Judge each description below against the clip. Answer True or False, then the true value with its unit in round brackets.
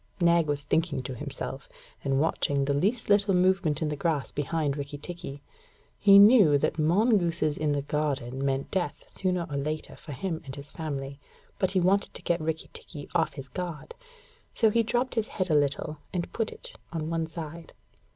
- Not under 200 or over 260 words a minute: False (190 wpm)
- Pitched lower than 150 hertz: False (160 Hz)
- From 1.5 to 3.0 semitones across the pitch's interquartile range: False (4.2 semitones)